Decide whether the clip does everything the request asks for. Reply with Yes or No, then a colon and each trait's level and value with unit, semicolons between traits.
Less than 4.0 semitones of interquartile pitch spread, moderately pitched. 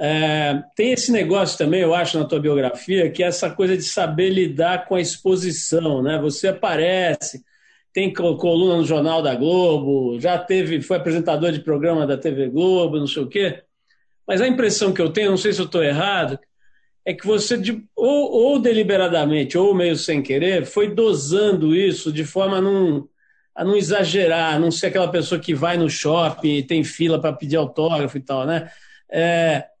Yes: average, 3.4 semitones; medium, 170 Hz